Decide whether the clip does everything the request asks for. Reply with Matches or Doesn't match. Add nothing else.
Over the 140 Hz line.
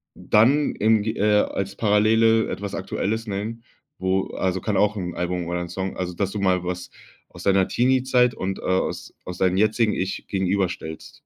Doesn't match